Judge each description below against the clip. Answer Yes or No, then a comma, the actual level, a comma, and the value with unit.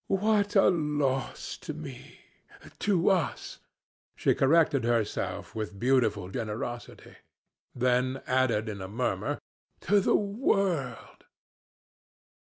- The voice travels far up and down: Yes, wide, 7.7 semitones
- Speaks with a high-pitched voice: No, low, 130 Hz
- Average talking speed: No, slow, 100 wpm